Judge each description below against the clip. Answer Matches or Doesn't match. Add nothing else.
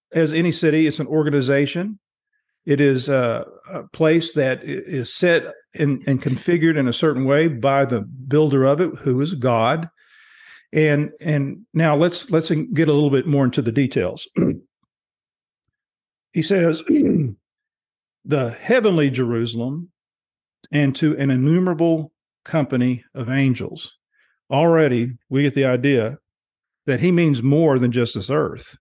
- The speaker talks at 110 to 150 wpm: Matches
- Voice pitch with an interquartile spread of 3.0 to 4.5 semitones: Matches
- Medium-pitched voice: Matches